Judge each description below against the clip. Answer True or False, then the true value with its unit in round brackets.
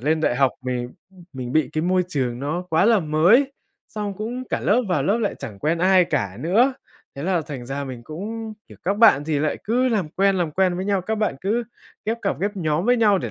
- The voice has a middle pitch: True (180 Hz)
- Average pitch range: False (6.0 semitones)